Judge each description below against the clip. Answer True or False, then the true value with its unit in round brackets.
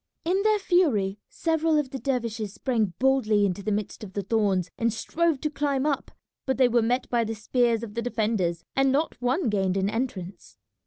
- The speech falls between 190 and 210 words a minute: True (200 wpm)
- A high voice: True (235 Hz)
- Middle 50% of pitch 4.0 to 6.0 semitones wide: True (4.7 semitones)